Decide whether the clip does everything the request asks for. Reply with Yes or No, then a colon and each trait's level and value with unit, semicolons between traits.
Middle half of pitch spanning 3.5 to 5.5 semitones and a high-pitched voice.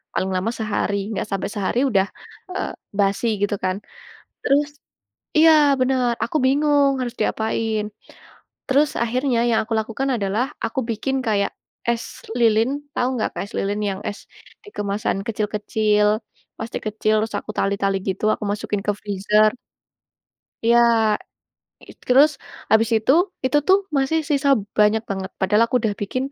Yes: average, 3.8 semitones; high, 220 Hz